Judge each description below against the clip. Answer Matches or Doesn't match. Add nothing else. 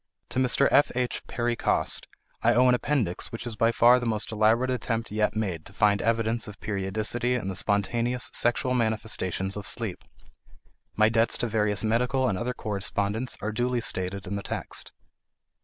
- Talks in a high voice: Doesn't match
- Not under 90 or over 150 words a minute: Doesn't match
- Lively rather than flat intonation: Doesn't match